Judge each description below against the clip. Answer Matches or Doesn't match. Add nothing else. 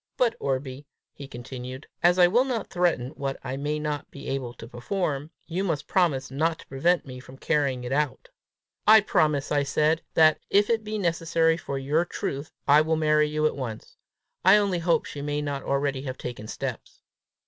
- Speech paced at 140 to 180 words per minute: Doesn't match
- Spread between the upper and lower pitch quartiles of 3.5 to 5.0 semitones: Matches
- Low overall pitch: Doesn't match